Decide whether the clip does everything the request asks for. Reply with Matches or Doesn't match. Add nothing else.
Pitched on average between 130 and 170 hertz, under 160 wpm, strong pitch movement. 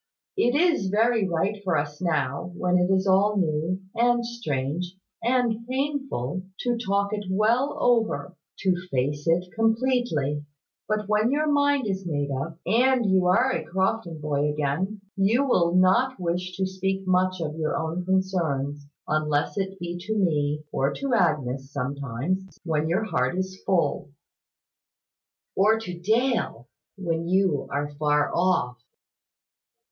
Doesn't match